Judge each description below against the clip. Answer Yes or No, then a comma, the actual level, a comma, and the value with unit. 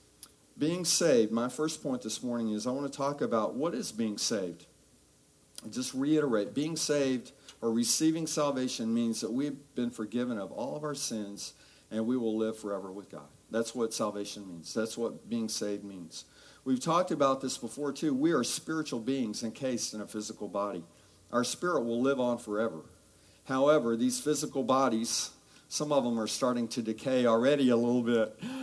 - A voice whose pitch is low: Yes, low, 120 Hz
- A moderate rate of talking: Yes, average, 180 wpm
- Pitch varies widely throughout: No, average, 4.2 semitones